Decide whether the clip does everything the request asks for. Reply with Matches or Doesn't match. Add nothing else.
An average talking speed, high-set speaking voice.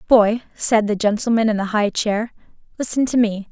Matches